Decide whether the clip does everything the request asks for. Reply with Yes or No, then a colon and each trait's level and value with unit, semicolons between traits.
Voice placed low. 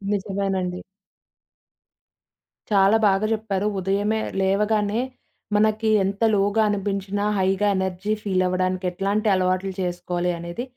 No: high, 195 Hz